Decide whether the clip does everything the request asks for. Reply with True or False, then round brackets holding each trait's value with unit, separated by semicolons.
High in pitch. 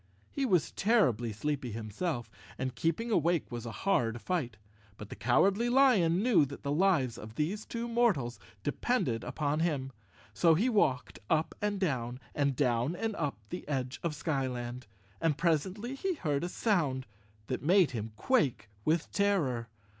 False (150 Hz)